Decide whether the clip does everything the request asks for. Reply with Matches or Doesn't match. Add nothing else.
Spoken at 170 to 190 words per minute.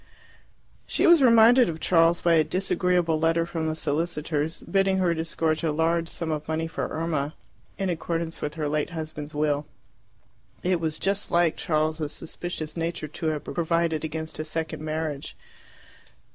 Doesn't match